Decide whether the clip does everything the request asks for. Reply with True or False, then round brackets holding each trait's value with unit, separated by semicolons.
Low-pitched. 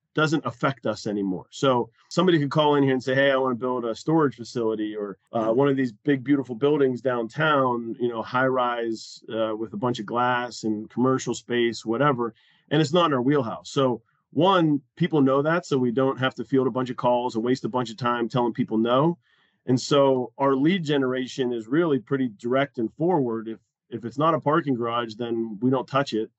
True (130 Hz)